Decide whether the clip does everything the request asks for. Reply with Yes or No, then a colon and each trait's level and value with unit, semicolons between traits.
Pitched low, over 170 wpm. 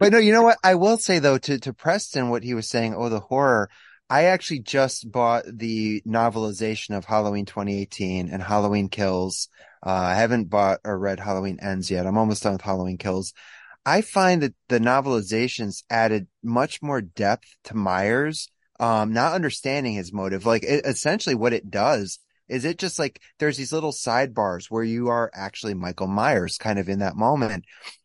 Yes: low, 115 Hz; average, 185 wpm